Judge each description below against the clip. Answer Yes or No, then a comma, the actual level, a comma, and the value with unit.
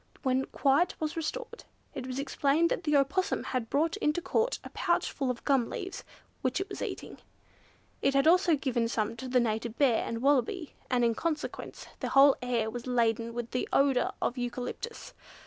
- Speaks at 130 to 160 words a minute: No, average, 185 wpm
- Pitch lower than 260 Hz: No, very high, 270 Hz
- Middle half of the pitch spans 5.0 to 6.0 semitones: No, average, 4.4 semitones